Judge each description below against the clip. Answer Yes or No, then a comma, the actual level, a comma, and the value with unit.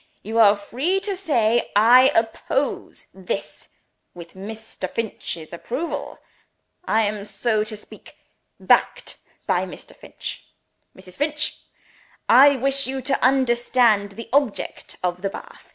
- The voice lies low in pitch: No, high, 230 Hz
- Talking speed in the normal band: No, slow, 125 wpm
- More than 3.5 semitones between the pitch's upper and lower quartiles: Yes, average, 4.8 semitones